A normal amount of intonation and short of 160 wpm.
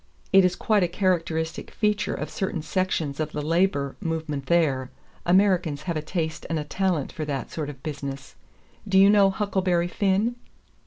No: average, 4.1 semitones; average, 170 wpm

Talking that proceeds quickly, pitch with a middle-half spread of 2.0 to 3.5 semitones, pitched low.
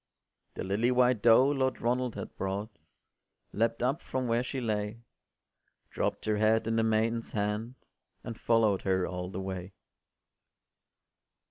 No: average, 140 wpm; average, 2.8 semitones; low, 115 Hz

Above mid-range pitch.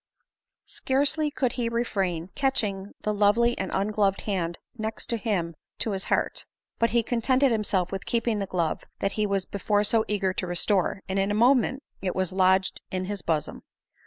Yes: high, 205 Hz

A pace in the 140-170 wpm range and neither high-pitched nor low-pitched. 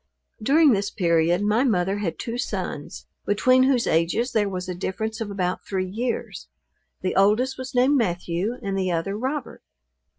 No: average, 165 wpm; high, 205 Hz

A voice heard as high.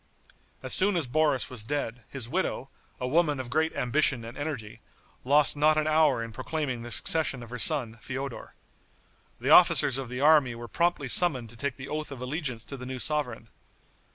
No: low, 135 Hz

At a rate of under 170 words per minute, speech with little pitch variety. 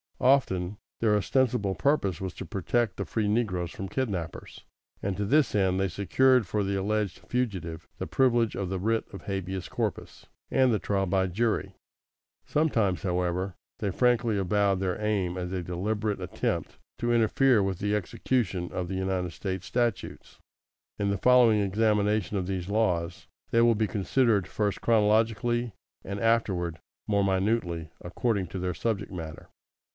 No: average, 155 wpm; average, 3.5 semitones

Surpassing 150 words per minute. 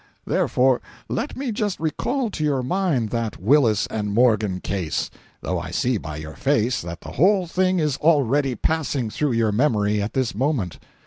Yes: average, 170 wpm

